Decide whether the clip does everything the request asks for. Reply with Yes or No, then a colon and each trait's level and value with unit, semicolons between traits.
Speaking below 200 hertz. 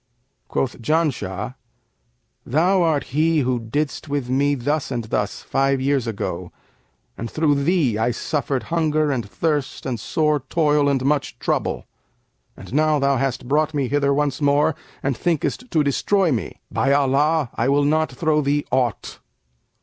Yes: medium, 140 Hz